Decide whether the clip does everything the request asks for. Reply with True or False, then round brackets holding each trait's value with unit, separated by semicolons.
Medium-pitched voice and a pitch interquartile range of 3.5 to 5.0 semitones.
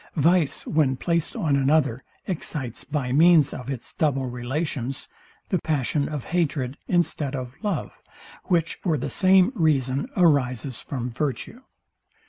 True (145 Hz; 4.2 semitones)